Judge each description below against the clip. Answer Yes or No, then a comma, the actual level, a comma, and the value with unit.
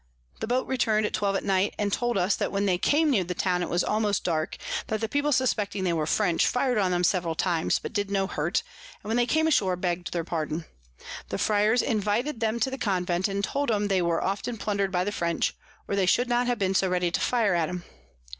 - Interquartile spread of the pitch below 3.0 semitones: No, average, 3.9 semitones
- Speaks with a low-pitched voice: No, high, 200 Hz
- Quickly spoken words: Yes, fast, 240 wpm